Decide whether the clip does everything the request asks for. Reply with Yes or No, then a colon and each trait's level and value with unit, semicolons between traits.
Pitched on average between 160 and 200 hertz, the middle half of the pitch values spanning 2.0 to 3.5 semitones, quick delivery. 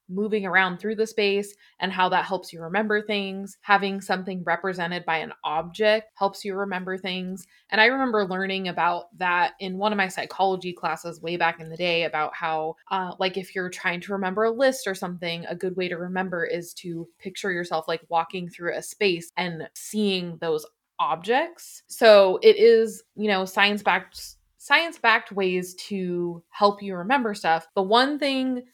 No: high, 190 Hz; average, 3.1 semitones; average, 185 wpm